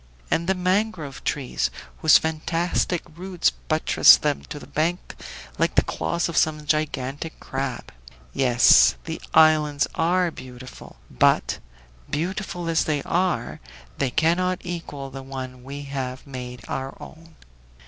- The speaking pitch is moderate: Yes, medium, 155 Hz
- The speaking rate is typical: No, slow, 130 wpm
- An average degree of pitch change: Yes, average, 4.1 semitones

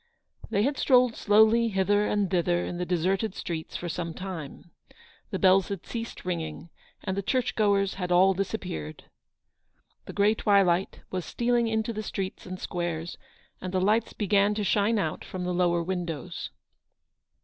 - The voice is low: No, high, 190 Hz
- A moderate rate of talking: Yes, average, 165 wpm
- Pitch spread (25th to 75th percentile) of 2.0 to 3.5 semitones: Yes, average, 3.0 semitones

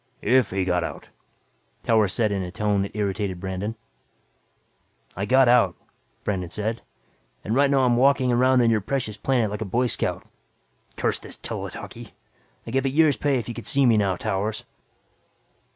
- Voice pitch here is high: No, low, 110 Hz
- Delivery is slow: No, average, 175 wpm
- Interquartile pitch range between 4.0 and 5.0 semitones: Yes, average, 4.4 semitones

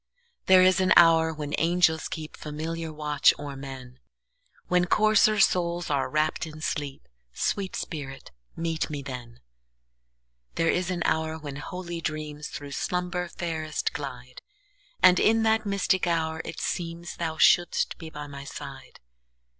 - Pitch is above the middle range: No, medium, 160 Hz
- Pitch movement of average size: Yes, average, 4.0 semitones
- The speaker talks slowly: Yes, slow, 120 wpm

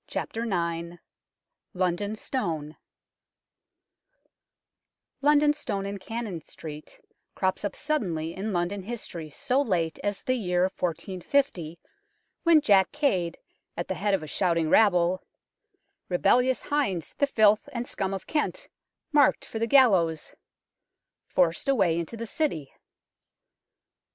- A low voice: No, high, 195 Hz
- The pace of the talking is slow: Yes, slow, 125 wpm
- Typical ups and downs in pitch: No, wide, 5.8 semitones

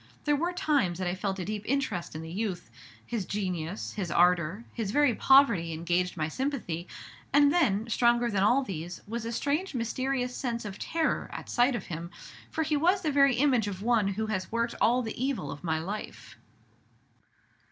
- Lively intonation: Yes, wide, 6.6 semitones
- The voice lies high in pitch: Yes, high, 225 Hz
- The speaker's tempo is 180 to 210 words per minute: Yes, average, 190 wpm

